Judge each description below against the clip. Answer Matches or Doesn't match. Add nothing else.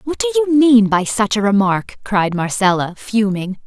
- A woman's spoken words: Matches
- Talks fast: Doesn't match